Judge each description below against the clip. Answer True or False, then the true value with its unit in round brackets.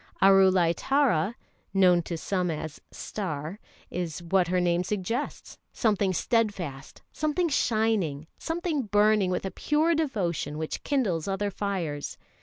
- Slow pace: True (125 wpm)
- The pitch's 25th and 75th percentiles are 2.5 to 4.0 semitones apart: False (4.7 semitones)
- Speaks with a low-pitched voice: False (195 Hz)